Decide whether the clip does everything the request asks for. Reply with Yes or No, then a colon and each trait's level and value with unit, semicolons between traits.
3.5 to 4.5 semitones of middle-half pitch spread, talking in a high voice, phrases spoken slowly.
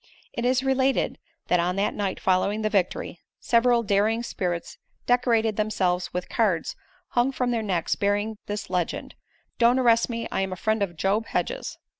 No: average, 3.8 semitones; high, 215 Hz; average, 170 wpm